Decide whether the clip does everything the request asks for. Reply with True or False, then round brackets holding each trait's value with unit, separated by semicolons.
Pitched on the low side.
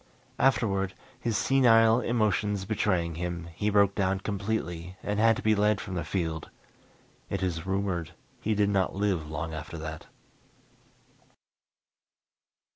True (95 Hz)